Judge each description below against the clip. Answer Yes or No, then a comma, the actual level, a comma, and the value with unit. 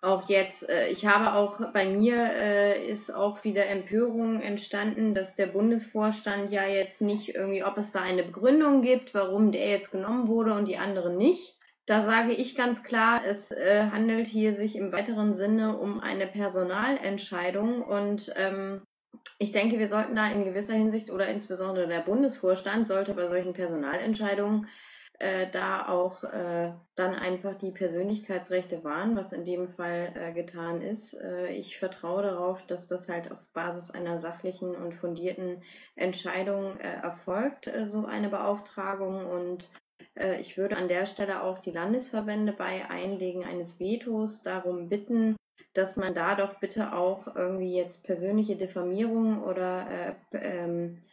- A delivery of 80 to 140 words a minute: No, average, 155 wpm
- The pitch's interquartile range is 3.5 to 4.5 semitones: No, average, 2.7 semitones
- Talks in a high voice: Yes, high, 195 Hz